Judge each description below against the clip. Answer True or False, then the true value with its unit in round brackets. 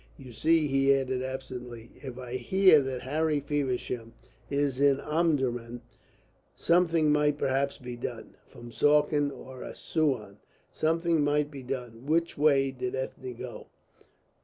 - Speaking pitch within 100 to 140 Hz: True (135 Hz)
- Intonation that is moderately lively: True (3.0 semitones)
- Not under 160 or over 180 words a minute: False (135 wpm)